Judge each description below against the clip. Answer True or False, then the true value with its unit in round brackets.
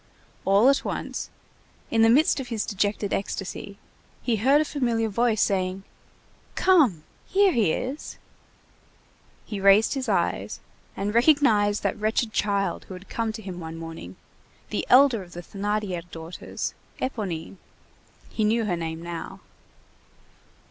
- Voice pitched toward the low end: False (210 Hz)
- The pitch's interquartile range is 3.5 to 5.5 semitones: True (4.2 semitones)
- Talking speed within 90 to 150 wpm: True (140 wpm)